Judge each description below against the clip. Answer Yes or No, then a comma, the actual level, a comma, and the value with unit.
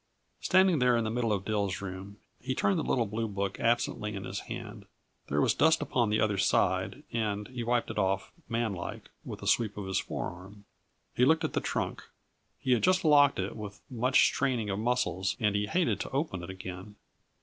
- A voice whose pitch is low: Yes, low, 110 Hz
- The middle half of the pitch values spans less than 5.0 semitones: Yes, average, 4.1 semitones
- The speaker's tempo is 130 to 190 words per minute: No, fast, 205 wpm